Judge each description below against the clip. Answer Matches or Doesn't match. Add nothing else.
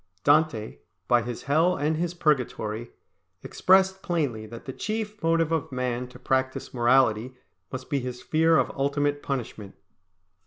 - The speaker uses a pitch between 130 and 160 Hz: Matches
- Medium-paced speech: Matches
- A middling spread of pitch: Matches